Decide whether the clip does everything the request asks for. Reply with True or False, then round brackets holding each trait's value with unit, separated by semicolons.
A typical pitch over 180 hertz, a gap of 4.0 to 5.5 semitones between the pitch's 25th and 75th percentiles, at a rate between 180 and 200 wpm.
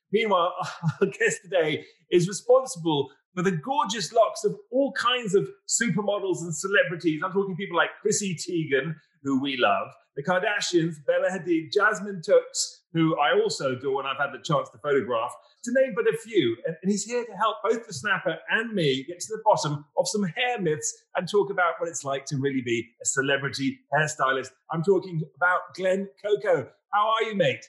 True (190 Hz; 5.2 semitones; 190 wpm)